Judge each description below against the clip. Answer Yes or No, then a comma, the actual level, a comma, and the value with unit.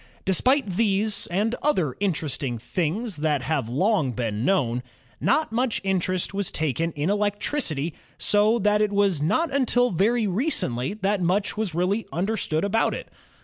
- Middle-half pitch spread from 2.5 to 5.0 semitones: No, wide, 5.5 semitones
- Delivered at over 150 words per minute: No, average, 145 wpm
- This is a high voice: Yes, high, 195 Hz